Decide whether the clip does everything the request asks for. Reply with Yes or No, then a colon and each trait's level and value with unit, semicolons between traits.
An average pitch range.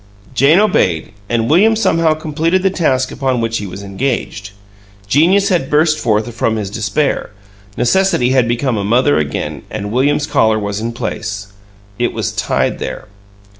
No: wide, 6.2 semitones